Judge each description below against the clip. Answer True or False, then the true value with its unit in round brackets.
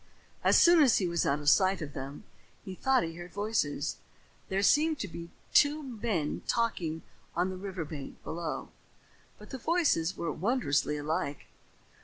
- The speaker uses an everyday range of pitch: False (6.6 semitones)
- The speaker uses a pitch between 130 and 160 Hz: False (180 Hz)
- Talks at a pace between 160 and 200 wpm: True (165 wpm)